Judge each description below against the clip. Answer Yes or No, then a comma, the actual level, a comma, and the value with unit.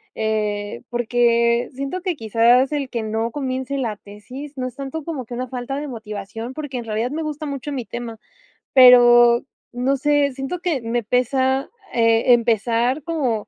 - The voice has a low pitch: No, high, 245 Hz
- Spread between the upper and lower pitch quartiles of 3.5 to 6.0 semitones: No, average, 3.1 semitones